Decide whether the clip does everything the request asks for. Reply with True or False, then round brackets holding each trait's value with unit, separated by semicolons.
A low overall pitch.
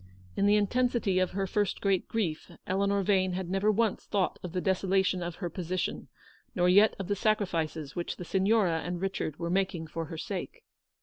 False (190 Hz)